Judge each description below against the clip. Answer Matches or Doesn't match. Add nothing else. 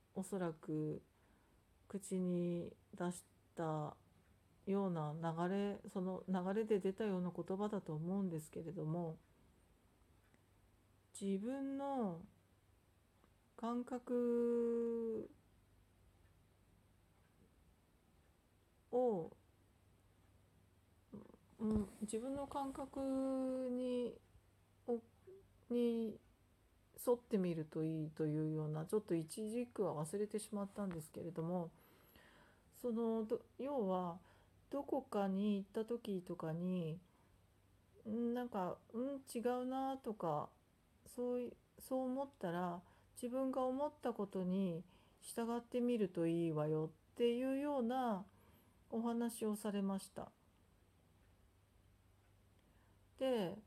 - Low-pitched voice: Doesn't match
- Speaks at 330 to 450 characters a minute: Doesn't match